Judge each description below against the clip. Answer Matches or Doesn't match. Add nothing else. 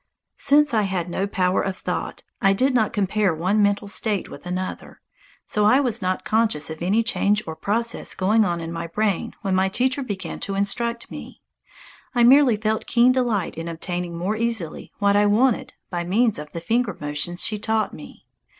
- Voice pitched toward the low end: Doesn't match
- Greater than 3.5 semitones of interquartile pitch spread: Matches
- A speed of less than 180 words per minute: Doesn't match